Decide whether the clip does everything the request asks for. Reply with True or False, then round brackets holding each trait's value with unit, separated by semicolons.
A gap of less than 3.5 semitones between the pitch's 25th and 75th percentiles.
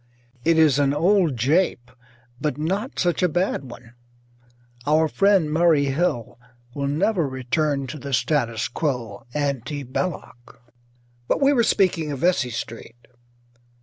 False (4.8 semitones)